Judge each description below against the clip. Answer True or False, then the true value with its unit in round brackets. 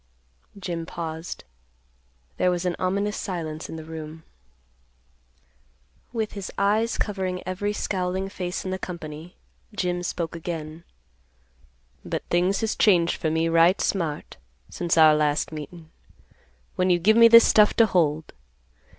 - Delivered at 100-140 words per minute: True (135 wpm)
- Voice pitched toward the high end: False (175 Hz)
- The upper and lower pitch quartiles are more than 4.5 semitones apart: False (3.1 semitones)